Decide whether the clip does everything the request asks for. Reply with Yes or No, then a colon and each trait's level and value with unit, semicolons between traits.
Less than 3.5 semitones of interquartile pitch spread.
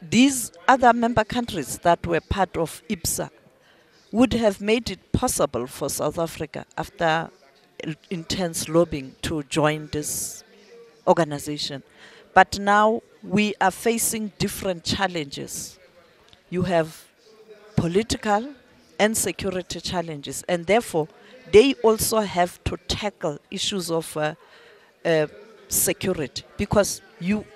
No: average, 4.7 semitones